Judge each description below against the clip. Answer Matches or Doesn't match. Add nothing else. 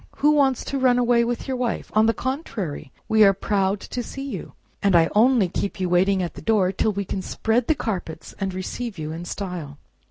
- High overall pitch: Matches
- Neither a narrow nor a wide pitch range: Matches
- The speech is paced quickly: Matches